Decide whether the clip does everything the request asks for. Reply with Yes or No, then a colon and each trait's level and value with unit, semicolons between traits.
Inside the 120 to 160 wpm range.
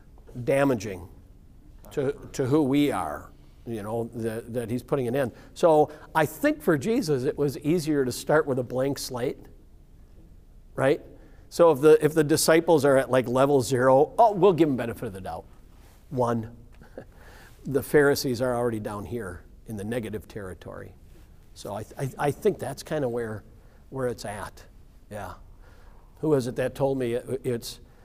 No: average, 170 wpm